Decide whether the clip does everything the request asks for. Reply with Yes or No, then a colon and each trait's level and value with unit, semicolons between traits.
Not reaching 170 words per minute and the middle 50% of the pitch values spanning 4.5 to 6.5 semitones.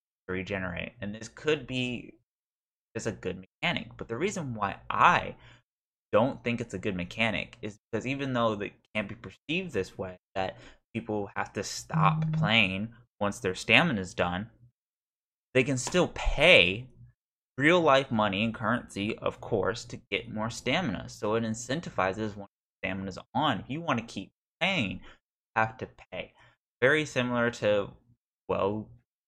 No: average, 160 wpm; average, 3.8 semitones